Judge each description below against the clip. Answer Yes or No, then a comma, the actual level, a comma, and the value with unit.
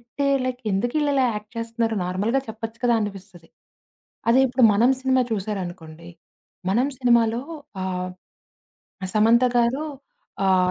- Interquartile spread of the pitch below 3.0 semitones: No, average, 4.4 semitones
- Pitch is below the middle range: No, high, 225 Hz